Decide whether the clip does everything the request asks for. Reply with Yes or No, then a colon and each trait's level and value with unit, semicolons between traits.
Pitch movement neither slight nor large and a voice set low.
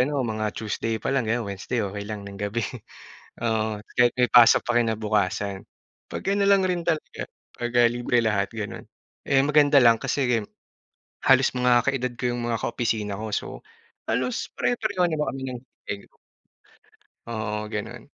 Yes: average, 3.0 semitones; low, 115 Hz